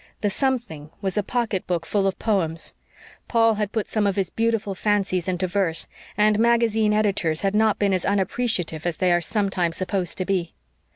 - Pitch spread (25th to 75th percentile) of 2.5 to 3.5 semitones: Yes, average, 3.0 semitones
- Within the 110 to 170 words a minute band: No, average, 180 wpm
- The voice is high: Yes, high, 200 Hz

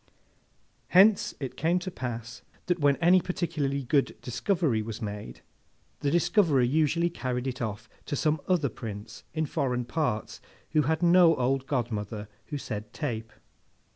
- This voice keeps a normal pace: Yes, average, 145 wpm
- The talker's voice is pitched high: No, medium, 140 Hz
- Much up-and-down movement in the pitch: Yes, wide, 5.8 semitones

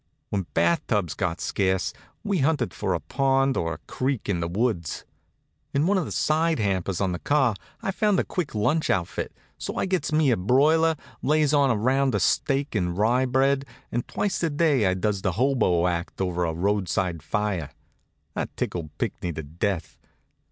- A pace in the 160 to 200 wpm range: Yes, average, 180 wpm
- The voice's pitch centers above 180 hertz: No, low, 110 Hz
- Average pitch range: No, wide, 7.9 semitones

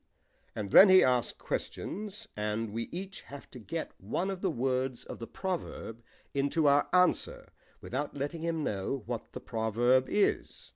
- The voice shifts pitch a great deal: Yes, wide, 6.9 semitones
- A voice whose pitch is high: No, low, 135 Hz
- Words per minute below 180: Yes, average, 160 wpm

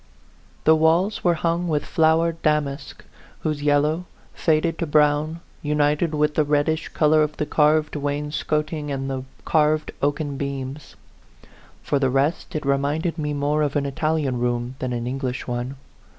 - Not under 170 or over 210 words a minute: No, average, 160 wpm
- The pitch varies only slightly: Yes, narrow, 2.0 semitones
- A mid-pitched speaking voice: Yes, medium, 150 Hz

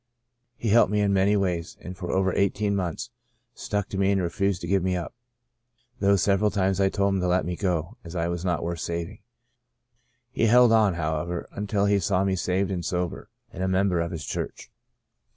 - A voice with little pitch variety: Yes, narrow, 2.3 semitones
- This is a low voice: Yes, very low, 95 Hz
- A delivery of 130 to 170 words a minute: No, fast, 205 wpm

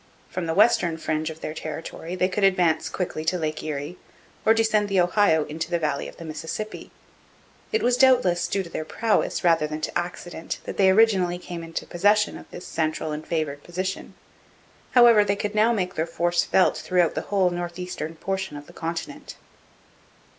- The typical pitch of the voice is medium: Yes, medium, 175 Hz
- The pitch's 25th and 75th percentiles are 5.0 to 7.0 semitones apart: No, average, 3.6 semitones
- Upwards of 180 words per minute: Yes, average, 190 wpm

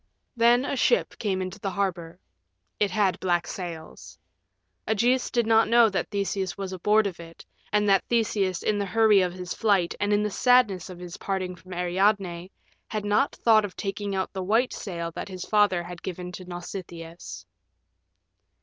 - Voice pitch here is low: No, high, 195 Hz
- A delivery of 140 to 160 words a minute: No, average, 175 wpm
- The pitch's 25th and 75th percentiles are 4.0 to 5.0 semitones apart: No, average, 2.8 semitones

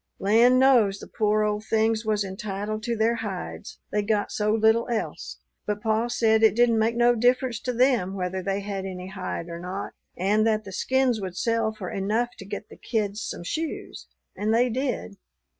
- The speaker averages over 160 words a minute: Yes, average, 190 wpm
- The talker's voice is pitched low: No, high, 215 Hz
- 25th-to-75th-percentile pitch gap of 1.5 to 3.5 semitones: Yes, average, 2.7 semitones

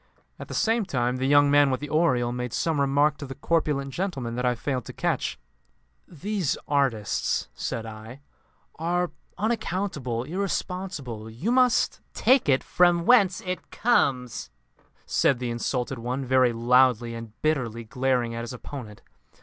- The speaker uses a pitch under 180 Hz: Yes, low, 135 Hz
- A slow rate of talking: No, average, 155 wpm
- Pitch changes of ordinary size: No, wide, 5.9 semitones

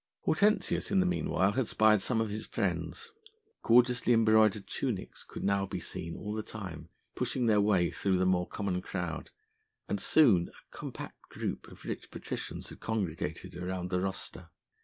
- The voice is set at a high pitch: No, low, 105 Hz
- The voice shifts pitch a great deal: No, average, 3.5 semitones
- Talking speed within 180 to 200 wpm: No, average, 165 wpm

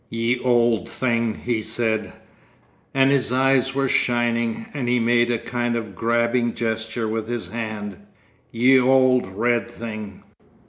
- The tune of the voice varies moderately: No, narrow, 1.7 semitones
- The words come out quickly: No, slow, 135 wpm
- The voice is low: Yes, low, 120 Hz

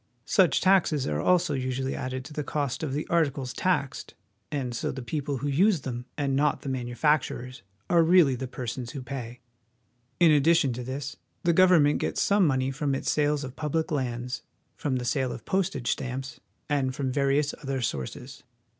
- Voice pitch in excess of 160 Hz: No, medium, 140 Hz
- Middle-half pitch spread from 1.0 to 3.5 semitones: Yes, average, 2.8 semitones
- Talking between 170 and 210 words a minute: Yes, average, 180 wpm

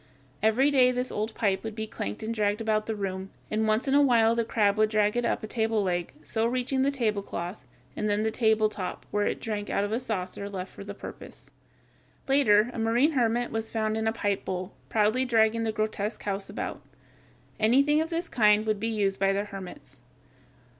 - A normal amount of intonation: No, narrow, 2.2 semitones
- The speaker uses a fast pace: Yes, fast, 210 wpm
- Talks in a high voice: Yes, high, 220 Hz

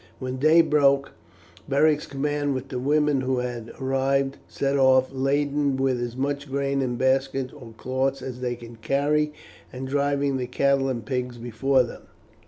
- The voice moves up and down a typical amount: No, narrow, 1.7 semitones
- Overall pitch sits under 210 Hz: Yes, low, 135 Hz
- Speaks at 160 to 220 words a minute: Yes, average, 165 wpm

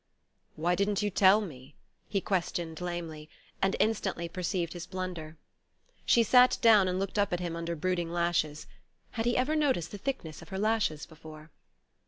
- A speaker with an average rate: Yes, average, 170 wpm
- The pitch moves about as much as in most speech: Yes, average, 3.8 semitones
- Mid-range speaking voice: Yes, medium, 180 Hz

